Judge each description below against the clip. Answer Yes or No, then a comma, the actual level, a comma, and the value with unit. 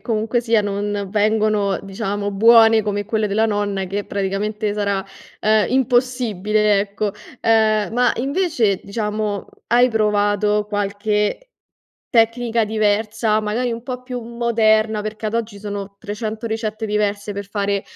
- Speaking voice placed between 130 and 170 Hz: No, high, 215 Hz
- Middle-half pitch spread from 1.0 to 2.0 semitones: Yes, narrow, 1.7 semitones